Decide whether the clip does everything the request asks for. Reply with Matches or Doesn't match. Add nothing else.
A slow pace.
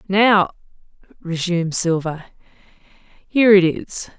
Matches